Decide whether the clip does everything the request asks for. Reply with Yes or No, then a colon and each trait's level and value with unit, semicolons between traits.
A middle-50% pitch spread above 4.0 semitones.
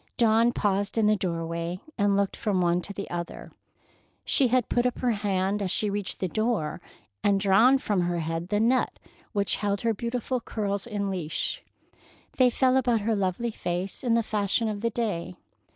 No: average, 3.6 semitones